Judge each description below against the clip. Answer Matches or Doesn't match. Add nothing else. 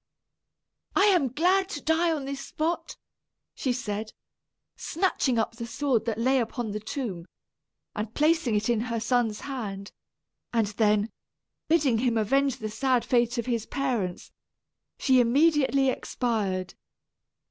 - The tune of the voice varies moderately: Matches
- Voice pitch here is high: Matches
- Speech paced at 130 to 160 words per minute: Matches